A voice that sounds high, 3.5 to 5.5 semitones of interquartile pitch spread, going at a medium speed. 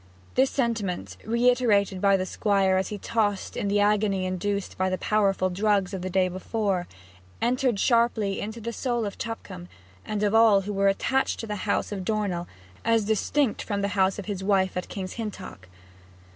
No: high, 205 Hz; average, 2.7 semitones; average, 185 wpm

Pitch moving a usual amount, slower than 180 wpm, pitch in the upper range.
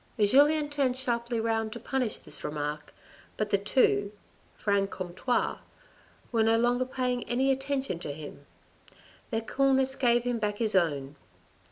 Yes: average, 4.3 semitones; average, 145 wpm; high, 235 Hz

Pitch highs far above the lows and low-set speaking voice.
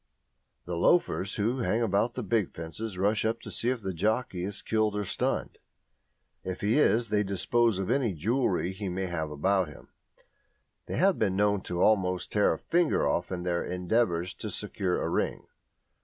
No: average, 3.8 semitones; low, 100 Hz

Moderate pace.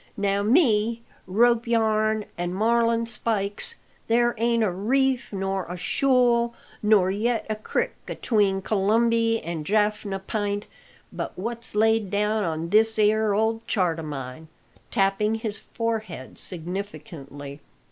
No: slow, 125 wpm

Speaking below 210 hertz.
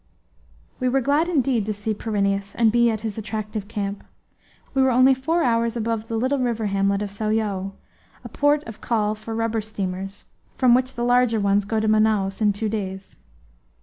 No: high, 220 Hz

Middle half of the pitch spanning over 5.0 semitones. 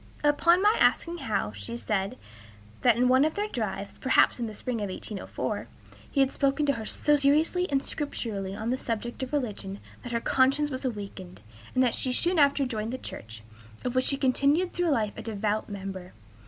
Yes: wide, 5.4 semitones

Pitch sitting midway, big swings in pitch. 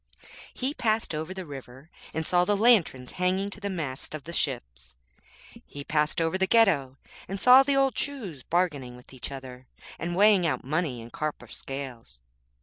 Yes: medium, 160 Hz; wide, 6.8 semitones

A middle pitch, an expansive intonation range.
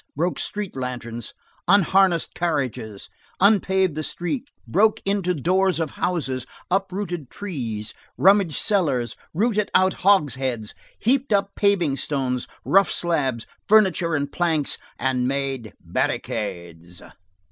Yes: medium, 165 Hz; wide, 7.0 semitones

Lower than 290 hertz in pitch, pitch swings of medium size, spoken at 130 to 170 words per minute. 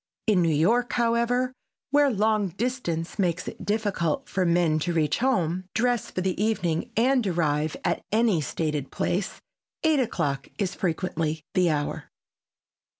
No: medium, 185 Hz; wide, 5.9 semitones; average, 145 wpm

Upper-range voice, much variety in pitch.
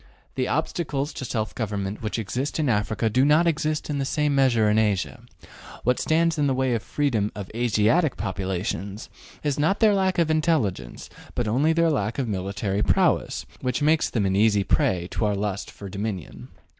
No: low, 120 Hz; wide, 6.4 semitones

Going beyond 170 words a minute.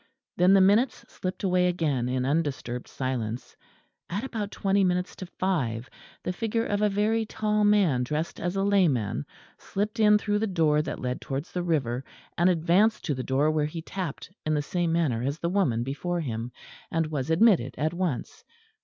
Yes: average, 185 wpm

